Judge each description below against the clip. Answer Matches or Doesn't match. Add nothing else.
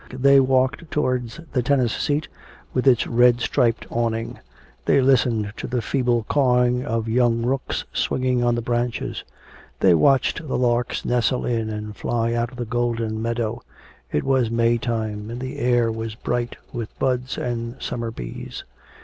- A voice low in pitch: Matches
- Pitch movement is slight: Matches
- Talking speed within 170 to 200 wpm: Doesn't match